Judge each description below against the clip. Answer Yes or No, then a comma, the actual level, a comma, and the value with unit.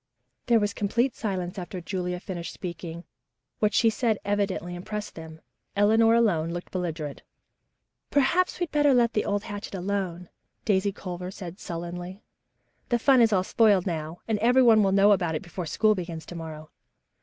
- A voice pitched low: No, high, 195 Hz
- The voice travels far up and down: No, average, 3.7 semitones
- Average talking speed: Yes, average, 165 wpm